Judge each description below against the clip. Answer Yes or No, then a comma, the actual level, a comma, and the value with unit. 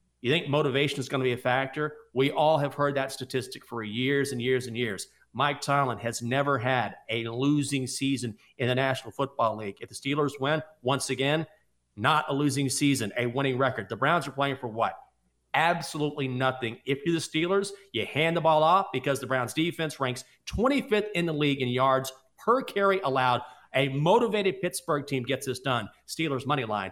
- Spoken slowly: No, average, 195 wpm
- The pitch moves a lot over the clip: No, average, 3.1 semitones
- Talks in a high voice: No, low, 135 Hz